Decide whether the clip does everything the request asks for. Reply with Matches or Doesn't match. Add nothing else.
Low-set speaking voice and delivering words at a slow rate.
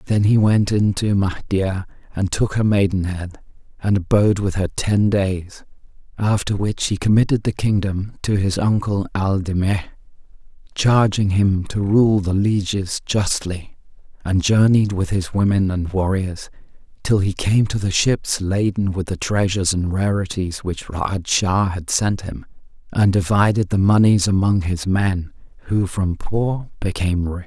Doesn't match